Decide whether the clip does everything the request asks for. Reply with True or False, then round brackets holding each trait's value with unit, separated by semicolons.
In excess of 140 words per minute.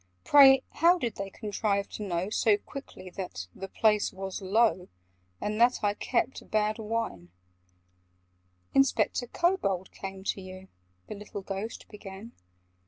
False (135 wpm)